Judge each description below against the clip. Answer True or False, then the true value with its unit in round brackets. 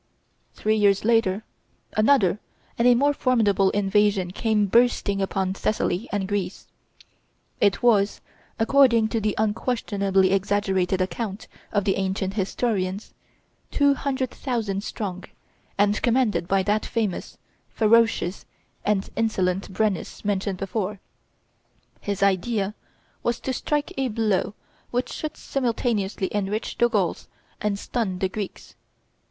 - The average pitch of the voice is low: False (205 Hz)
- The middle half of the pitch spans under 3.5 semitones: True (2.9 semitones)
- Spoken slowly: True (120 wpm)